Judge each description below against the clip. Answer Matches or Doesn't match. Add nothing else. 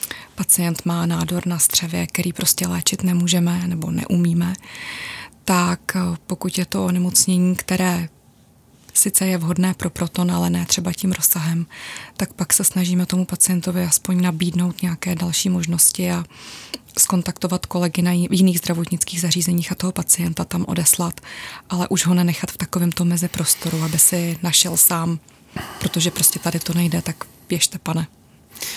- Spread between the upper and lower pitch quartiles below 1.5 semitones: Matches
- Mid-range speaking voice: Matches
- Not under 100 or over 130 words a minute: Doesn't match